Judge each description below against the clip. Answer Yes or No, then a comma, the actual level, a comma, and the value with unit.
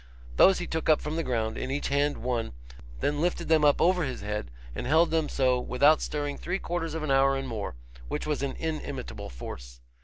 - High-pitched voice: No, medium, 145 Hz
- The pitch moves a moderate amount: Yes, average, 4.3 semitones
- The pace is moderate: No, fast, 215 wpm